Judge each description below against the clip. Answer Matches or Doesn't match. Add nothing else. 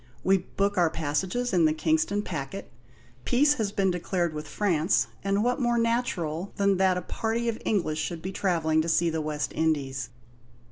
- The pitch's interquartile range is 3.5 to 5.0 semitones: Matches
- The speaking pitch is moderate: Matches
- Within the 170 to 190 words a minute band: Matches